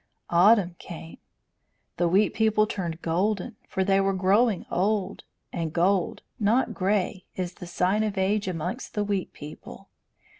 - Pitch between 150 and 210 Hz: Yes, high, 190 Hz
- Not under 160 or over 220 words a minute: No, average, 145 wpm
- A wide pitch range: No, average, 2.9 semitones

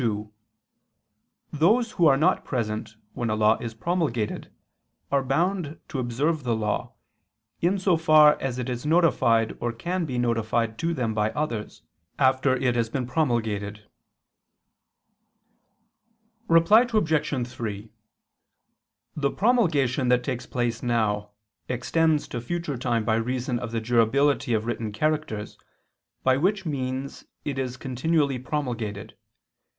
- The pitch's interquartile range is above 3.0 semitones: Yes, average, 5.0 semitones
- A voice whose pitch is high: No, low, 130 Hz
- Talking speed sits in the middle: No, slow, 130 wpm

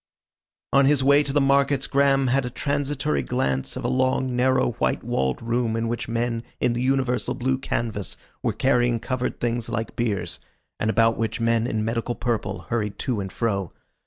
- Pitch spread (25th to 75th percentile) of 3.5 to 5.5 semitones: No, narrow, 2.6 semitones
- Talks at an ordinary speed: Yes, average, 185 wpm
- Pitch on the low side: Yes, low, 120 Hz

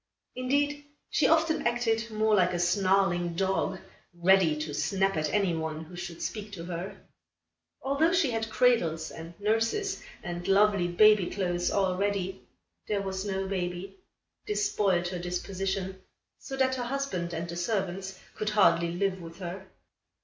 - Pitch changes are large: No, average, 3.8 semitones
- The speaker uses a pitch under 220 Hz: Yes, high, 190 Hz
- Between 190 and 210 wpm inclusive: No, average, 155 wpm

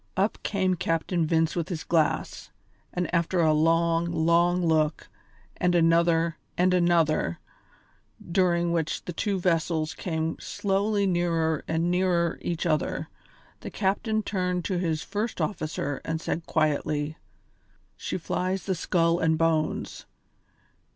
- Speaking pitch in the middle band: Yes, medium, 170 Hz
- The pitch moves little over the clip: Yes, narrow, 2.0 semitones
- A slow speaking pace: Yes, slow, 130 wpm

